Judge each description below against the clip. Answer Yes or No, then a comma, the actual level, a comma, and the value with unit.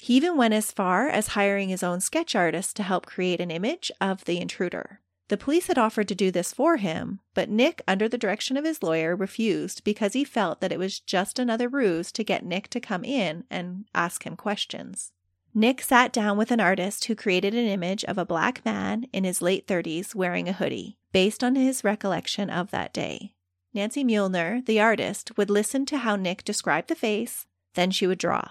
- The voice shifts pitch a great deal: No, average, 4.1 semitones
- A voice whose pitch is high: Yes, high, 205 Hz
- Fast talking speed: Yes, fast, 210 wpm